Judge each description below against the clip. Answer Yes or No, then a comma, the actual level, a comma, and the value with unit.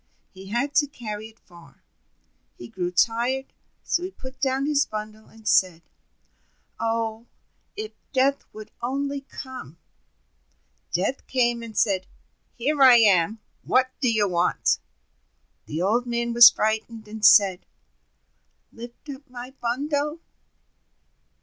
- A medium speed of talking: No, slow, 125 wpm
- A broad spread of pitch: No, average, 3.8 semitones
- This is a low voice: No, high, 235 Hz